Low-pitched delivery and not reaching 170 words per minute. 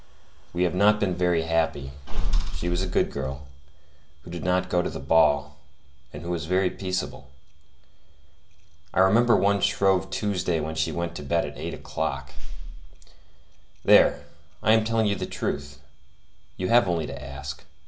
Yes: very low, 85 Hz; average, 160 wpm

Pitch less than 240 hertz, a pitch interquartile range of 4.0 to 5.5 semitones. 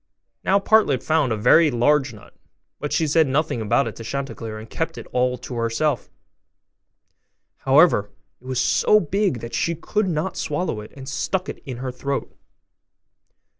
Yes: low, 135 Hz; average, 5.2 semitones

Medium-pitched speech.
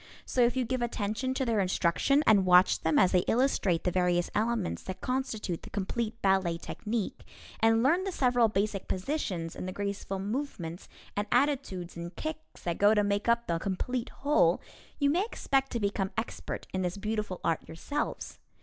No: high, 210 Hz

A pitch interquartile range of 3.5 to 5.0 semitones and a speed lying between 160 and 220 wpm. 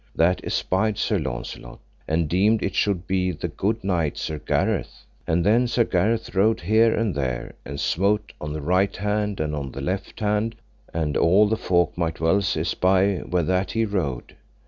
Yes: average, 4.2 semitones; average, 180 wpm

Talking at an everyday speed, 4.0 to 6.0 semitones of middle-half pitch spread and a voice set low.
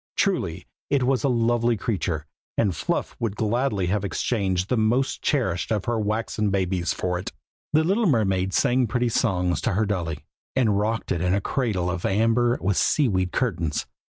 Yes: average, 180 wpm; average, 4.5 semitones; low, 105 Hz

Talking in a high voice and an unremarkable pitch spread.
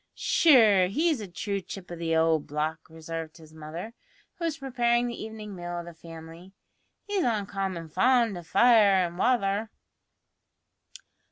No: high, 195 Hz; wide, 6.2 semitones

